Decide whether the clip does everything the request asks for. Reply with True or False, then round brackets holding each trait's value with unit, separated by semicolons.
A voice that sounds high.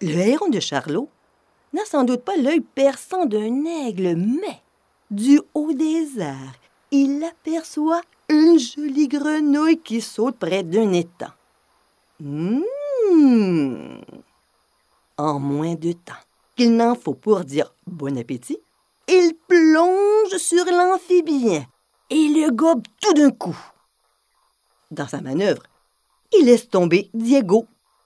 True (275 Hz)